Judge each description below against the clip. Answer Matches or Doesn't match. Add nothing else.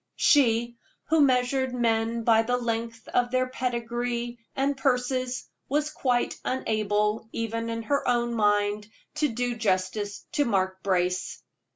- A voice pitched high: Matches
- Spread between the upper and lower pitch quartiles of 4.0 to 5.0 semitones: Doesn't match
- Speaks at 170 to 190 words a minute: Doesn't match